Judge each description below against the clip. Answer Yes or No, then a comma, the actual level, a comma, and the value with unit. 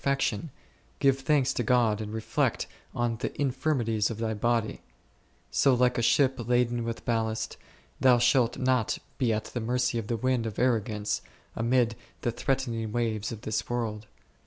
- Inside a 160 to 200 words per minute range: Yes, average, 165 wpm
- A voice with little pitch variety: Yes, narrow, 2.3 semitones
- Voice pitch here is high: No, low, 120 Hz